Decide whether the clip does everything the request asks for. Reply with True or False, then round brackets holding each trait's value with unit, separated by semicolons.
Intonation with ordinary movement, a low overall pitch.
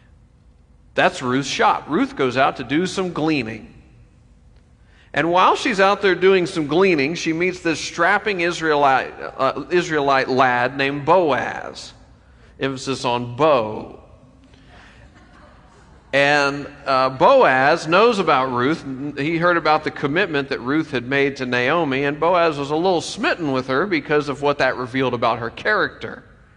False (4.1 semitones; 145 Hz)